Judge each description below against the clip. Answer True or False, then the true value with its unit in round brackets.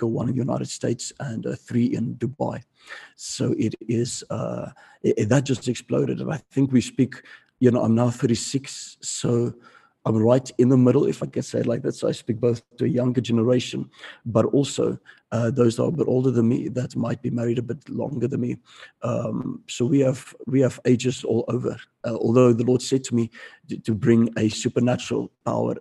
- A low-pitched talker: True (120 Hz)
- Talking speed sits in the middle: False (210 wpm)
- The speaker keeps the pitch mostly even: True (1.5 semitones)